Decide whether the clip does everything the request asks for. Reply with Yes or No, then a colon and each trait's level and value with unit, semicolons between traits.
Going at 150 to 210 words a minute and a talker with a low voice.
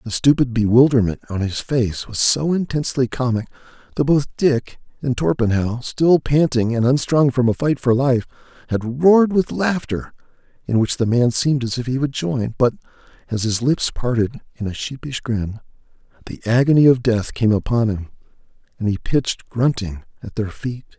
Yes: average, 175 wpm; low, 125 Hz